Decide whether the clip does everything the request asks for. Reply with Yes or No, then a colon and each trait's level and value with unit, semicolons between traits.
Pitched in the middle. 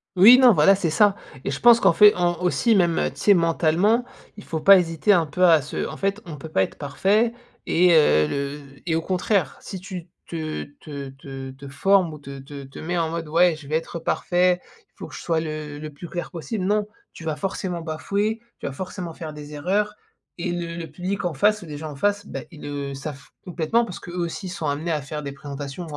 Yes: medium, 165 Hz